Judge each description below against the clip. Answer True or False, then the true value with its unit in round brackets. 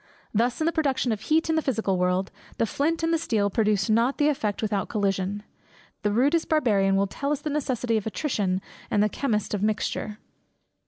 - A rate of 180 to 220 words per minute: True (200 wpm)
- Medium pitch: False (220 Hz)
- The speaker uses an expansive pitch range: True (5.9 semitones)